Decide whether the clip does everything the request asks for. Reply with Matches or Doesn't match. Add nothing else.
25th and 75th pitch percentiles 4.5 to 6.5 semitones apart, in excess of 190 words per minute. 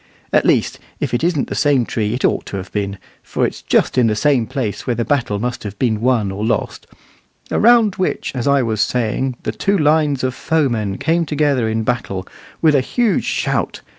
Matches